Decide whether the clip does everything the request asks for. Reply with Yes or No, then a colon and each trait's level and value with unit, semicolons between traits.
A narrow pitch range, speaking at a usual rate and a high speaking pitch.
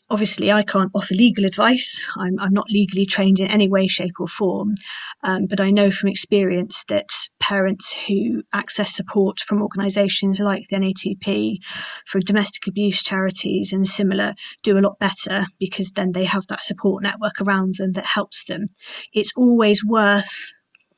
Yes: narrow, 1.3 semitones; average, 165 wpm; high, 200 Hz